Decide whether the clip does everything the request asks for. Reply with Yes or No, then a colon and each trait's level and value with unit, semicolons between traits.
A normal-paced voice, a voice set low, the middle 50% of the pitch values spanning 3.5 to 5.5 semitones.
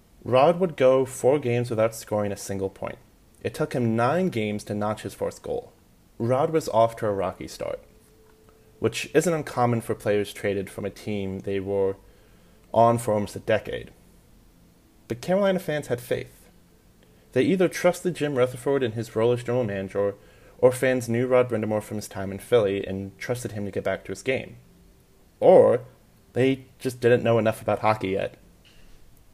Yes: average, 175 wpm; low, 115 Hz; average, 4.4 semitones